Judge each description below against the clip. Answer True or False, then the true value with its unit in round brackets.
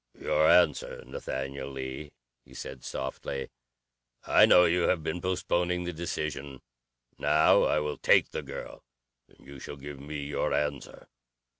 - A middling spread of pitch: True (3.7 semitones)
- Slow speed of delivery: False (145 wpm)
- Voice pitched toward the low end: True (75 Hz)